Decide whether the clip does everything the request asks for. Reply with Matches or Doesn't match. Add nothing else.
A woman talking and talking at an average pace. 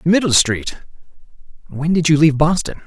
Doesn't match